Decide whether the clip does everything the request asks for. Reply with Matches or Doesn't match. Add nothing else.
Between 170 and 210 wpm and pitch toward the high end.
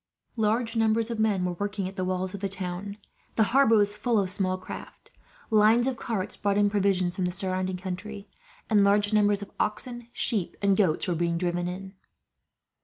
Matches